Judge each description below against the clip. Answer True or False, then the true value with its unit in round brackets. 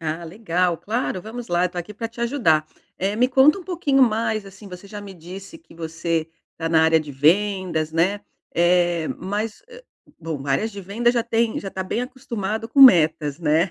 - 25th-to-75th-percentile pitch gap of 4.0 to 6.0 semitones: True (5.4 semitones)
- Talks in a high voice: True (195 Hz)